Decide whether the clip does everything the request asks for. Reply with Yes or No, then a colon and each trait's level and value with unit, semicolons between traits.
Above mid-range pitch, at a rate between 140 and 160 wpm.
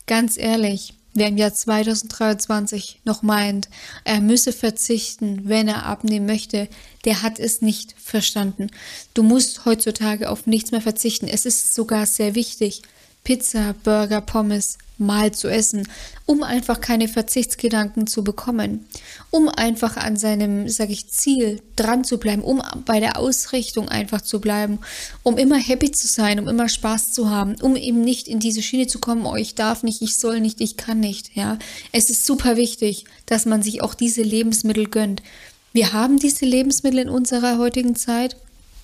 No: high, 225 Hz; average, 170 wpm